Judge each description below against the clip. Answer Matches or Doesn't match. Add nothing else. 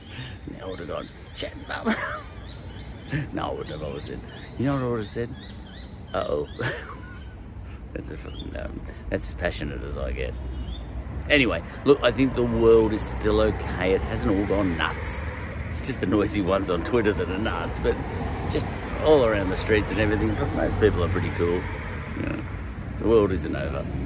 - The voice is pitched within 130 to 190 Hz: Doesn't match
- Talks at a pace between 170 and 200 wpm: Matches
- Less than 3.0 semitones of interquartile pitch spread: Doesn't match